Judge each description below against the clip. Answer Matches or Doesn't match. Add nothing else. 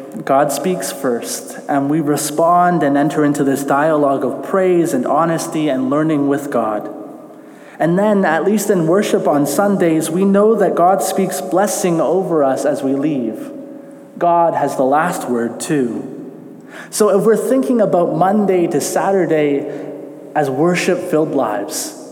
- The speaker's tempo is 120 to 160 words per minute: Matches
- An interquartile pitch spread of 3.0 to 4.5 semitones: Doesn't match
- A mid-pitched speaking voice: Matches